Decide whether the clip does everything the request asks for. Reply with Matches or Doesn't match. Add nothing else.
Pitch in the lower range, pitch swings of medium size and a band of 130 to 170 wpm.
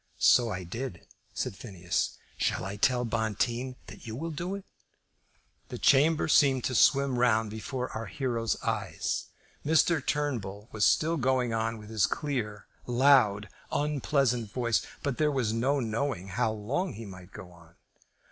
Matches